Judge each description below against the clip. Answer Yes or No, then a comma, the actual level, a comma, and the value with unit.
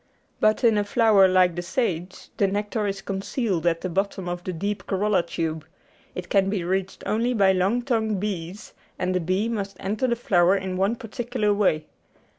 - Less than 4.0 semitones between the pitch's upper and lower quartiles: Yes, average, 2.7 semitones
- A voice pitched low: No, high, 195 Hz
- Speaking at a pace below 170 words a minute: No, average, 190 wpm